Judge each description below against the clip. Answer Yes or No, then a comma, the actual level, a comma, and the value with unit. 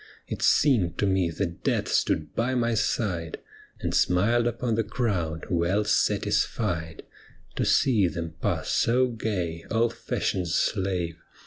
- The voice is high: No, very low, 95 Hz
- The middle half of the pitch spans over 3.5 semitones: Yes, wide, 5.5 semitones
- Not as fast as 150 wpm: Yes, slow, 135 wpm